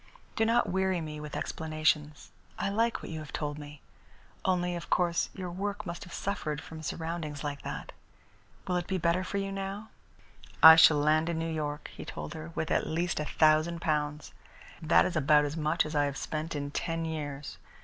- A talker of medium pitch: Yes, medium, 160 Hz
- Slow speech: No, average, 200 wpm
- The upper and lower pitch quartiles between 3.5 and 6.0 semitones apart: No, average, 2.8 semitones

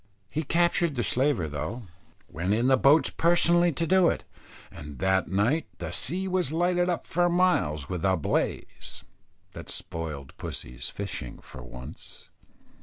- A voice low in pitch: Yes, low, 130 Hz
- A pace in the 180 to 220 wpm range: No, average, 150 wpm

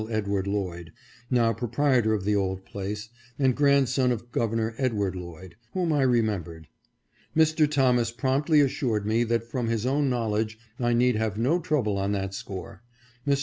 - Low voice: Yes, low, 115 Hz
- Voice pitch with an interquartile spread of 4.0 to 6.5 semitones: Yes, average, 4.5 semitones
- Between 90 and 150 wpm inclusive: No, average, 160 wpm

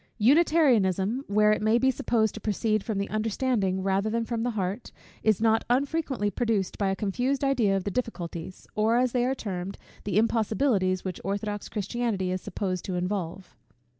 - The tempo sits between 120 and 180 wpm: Yes, average, 175 wpm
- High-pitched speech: Yes, high, 215 Hz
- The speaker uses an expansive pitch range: No, average, 3.8 semitones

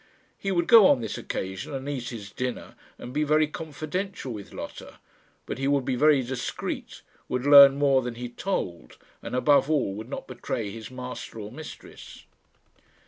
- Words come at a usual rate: Yes, average, 175 wpm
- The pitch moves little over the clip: No, average, 3.6 semitones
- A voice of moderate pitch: No, low, 130 Hz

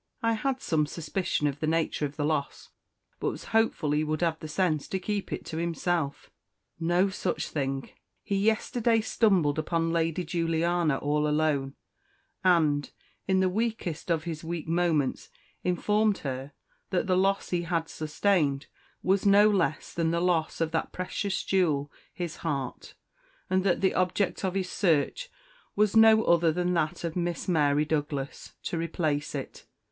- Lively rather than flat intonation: No, average, 3.5 semitones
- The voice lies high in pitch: No, medium, 170 Hz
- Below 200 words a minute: Yes, average, 160 wpm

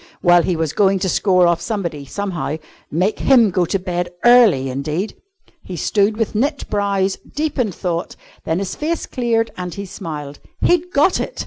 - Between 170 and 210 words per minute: Yes, average, 180 wpm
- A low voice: No, high, 190 Hz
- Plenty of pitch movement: No, average, 4.7 semitones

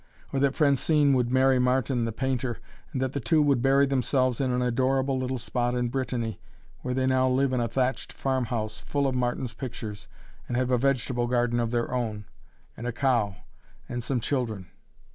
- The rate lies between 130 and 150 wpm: No, average, 195 wpm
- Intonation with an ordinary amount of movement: No, narrow, 1.9 semitones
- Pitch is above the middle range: No, low, 125 Hz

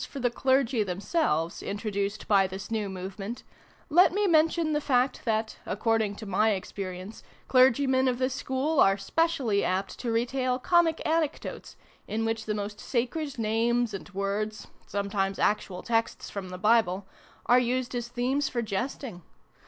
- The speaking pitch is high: Yes, high, 225 Hz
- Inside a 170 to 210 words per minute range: No, average, 155 wpm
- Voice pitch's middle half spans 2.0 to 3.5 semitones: No, average, 4.6 semitones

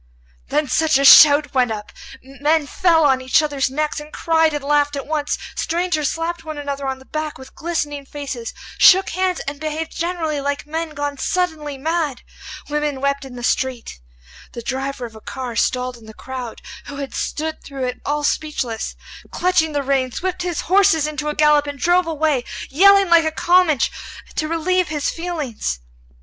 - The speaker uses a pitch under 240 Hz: No, very high, 295 Hz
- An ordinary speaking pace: Yes, average, 180 wpm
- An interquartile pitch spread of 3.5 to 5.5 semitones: No, average, 3.0 semitones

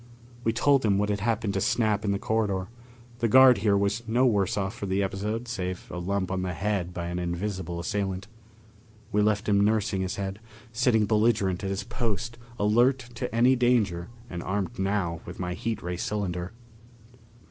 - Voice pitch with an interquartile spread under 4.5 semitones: Yes, average, 3.1 semitones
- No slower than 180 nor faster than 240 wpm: Yes, average, 185 wpm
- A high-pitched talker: No, low, 100 Hz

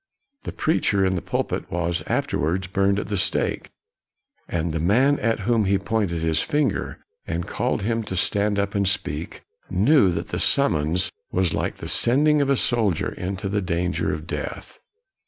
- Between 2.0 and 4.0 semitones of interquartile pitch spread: No, average, 4.5 semitones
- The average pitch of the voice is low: Yes, very low, 95 Hz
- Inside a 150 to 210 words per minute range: Yes, average, 175 wpm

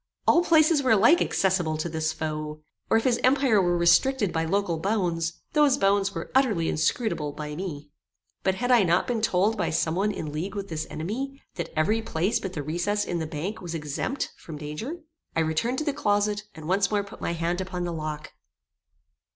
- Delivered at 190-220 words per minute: Yes, average, 200 wpm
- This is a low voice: No, high, 190 Hz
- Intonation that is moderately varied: No, wide, 5.7 semitones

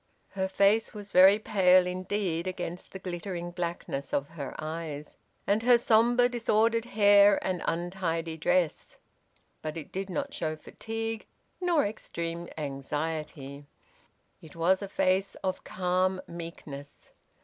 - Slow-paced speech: Yes, slow, 125 wpm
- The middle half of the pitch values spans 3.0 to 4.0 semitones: Yes, average, 3.7 semitones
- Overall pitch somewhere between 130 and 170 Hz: No, medium, 185 Hz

